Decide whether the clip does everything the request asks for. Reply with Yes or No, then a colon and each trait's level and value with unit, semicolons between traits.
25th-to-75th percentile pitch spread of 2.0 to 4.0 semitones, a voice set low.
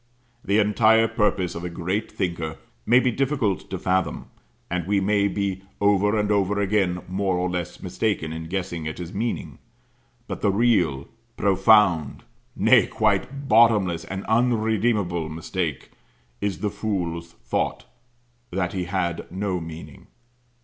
Yes: average, 3.2 semitones; very low, 95 Hz